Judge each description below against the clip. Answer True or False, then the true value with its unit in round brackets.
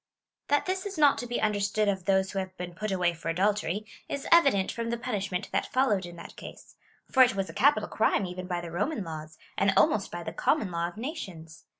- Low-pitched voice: False (195 Hz)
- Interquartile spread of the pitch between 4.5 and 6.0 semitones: True (4.9 semitones)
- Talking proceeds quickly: True (230 wpm)